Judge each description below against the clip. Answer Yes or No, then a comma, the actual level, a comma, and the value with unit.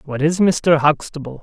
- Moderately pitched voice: Yes, medium, 150 Hz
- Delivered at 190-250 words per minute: No, average, 170 wpm